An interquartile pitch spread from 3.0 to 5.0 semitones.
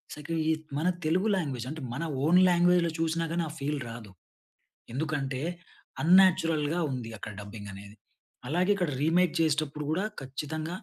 Yes: average, 3.9 semitones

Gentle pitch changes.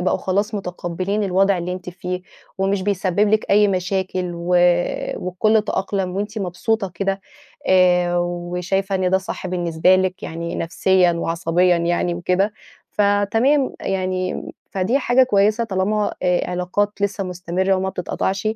Yes: narrow, 2.0 semitones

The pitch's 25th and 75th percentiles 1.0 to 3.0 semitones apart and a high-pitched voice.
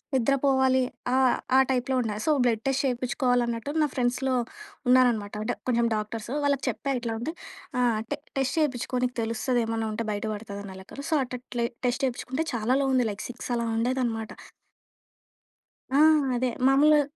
Yes: narrow, 2.5 semitones; high, 245 Hz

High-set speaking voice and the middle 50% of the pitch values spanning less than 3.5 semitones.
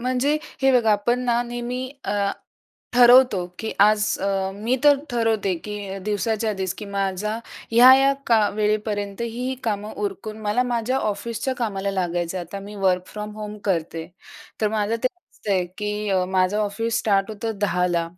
Yes: high, 210 Hz; average, 2.9 semitones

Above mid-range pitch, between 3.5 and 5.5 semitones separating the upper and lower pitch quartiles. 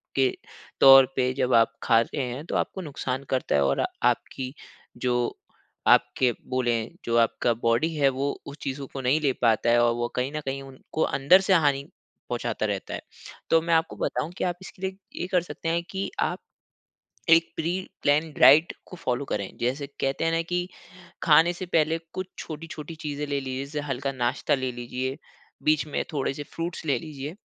No: medium, 140 Hz; average, 4.3 semitones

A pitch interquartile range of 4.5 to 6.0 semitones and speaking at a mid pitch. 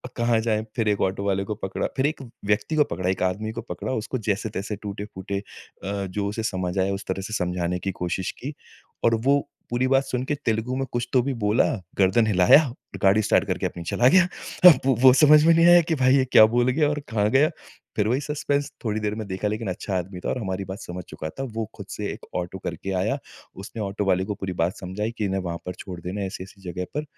No: average, 5.0 semitones; low, 105 Hz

